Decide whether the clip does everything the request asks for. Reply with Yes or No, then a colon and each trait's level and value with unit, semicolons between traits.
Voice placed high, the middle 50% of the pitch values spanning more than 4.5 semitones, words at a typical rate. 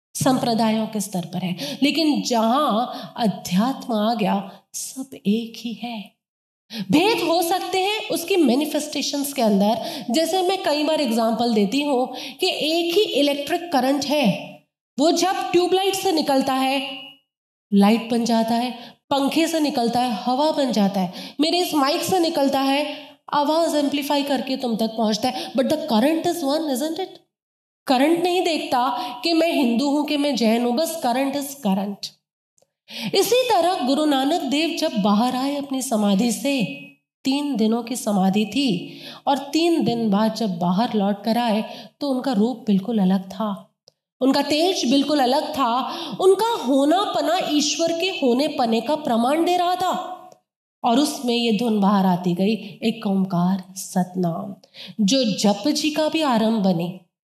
Yes: very high, 265 Hz; wide, 5.6 semitones; average, 160 wpm